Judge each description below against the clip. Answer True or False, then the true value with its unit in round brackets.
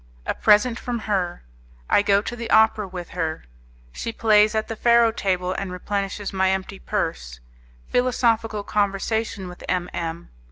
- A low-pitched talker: False (205 Hz)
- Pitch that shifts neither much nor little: True (3.3 semitones)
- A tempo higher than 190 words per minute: False (155 wpm)